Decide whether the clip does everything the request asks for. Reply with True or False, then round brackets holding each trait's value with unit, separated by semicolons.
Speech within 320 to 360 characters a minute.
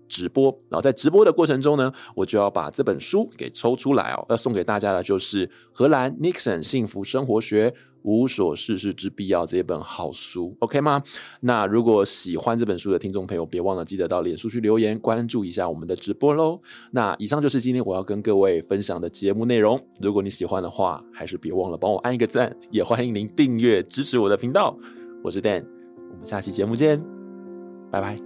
True (330 characters per minute)